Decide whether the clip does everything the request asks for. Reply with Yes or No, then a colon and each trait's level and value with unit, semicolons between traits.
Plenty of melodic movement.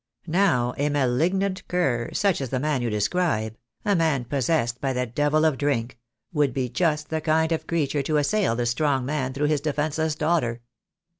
No: average, 4.2 semitones